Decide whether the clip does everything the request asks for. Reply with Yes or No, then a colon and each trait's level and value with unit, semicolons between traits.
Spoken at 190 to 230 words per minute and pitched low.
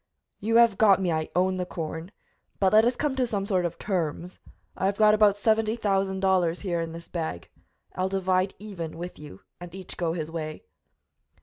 No: average, 200 wpm; medium, 185 Hz